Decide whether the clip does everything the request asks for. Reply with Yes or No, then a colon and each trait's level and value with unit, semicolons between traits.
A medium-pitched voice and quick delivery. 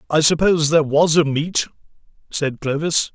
No: medium, 155 Hz; average, 155 wpm